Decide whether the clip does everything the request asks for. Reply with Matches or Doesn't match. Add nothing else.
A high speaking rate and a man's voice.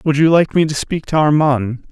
Matches